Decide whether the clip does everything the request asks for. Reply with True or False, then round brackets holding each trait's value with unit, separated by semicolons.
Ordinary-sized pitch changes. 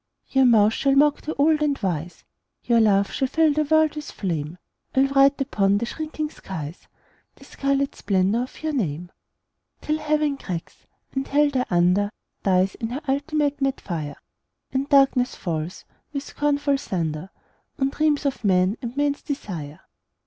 False (7.3 semitones)